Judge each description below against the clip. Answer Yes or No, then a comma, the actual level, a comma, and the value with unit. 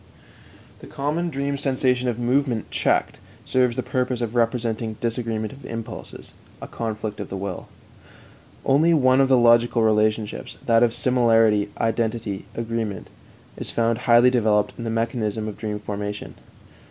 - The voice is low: Yes, low, 115 Hz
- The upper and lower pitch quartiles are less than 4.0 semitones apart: Yes, narrow, 2.6 semitones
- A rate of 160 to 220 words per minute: No, average, 145 wpm